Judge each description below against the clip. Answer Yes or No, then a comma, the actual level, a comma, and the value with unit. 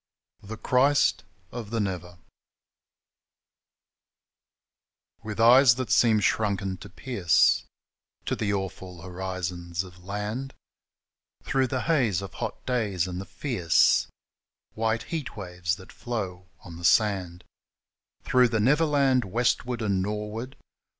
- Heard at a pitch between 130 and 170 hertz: No, low, 105 Hz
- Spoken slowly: Yes, slow, 125 wpm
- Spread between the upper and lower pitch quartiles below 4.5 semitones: No, average, 4.9 semitones